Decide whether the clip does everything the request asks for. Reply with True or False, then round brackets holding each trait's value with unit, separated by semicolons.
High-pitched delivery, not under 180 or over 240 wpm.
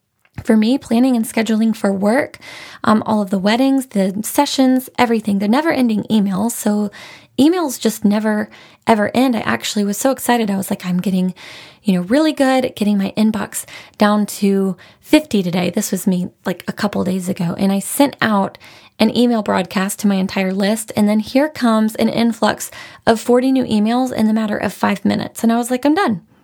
True (215 Hz; 195 wpm)